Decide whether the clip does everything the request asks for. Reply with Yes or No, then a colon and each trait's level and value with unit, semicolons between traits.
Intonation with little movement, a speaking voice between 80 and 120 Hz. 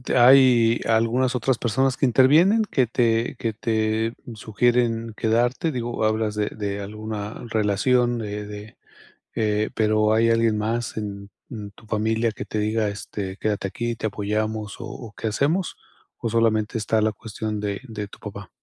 Yes: narrow, 2.0 semitones; low, 110 Hz